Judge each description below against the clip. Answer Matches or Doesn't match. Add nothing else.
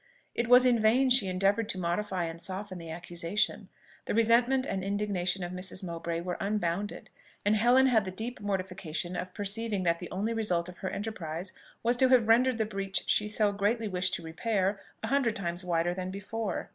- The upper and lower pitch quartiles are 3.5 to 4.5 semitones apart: Matches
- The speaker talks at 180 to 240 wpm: Matches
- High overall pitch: Matches